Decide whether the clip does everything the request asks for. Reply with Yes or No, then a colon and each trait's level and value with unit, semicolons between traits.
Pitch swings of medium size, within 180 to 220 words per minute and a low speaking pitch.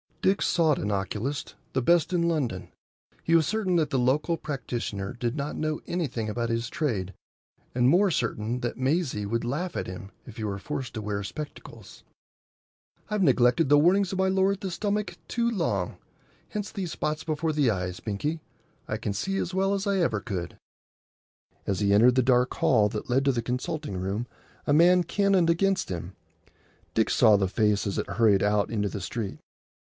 No: wide, 8.3 semitones; average, 185 wpm; low, 130 Hz